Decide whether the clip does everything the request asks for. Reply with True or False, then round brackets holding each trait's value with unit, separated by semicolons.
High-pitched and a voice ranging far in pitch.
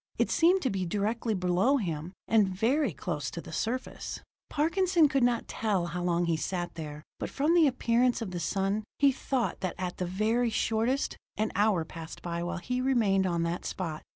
True (200 Hz; 6.1 semitones)